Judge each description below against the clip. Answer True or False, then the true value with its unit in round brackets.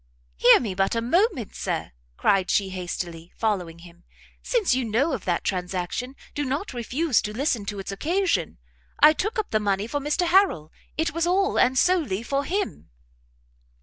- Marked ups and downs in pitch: True (9.0 semitones)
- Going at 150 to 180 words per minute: True (175 wpm)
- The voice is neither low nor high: False (240 Hz)